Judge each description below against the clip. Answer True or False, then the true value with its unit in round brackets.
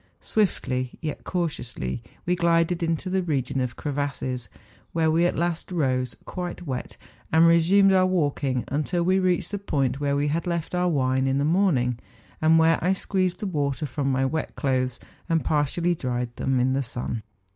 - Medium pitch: True (155 Hz)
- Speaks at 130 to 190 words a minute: True (180 wpm)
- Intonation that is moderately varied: True (4.8 semitones)